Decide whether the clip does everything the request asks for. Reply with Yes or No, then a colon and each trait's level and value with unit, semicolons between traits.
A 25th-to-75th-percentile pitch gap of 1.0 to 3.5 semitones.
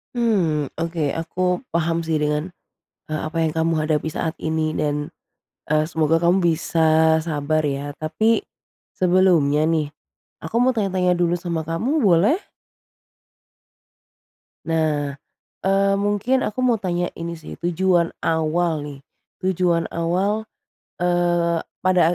Yes: average, 2.8 semitones